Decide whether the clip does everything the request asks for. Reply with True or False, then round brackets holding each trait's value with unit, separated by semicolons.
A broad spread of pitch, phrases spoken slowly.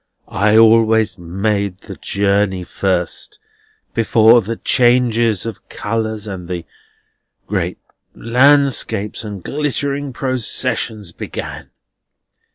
False (3.3 semitones; 90 wpm)